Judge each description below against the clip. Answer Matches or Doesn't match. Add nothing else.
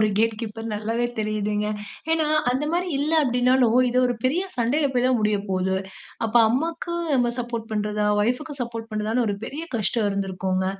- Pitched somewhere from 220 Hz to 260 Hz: Matches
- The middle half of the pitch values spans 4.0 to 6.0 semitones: Doesn't match